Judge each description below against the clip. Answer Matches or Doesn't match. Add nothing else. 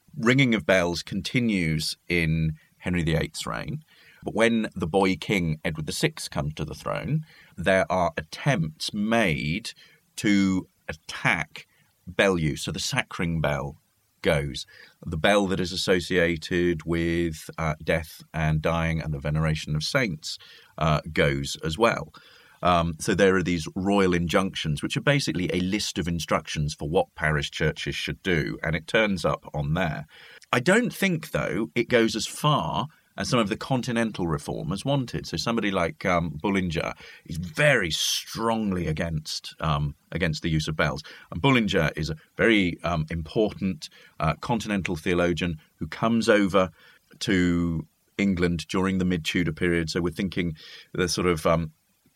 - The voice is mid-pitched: Doesn't match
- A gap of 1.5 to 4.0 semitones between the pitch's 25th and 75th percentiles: Doesn't match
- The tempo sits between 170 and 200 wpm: Doesn't match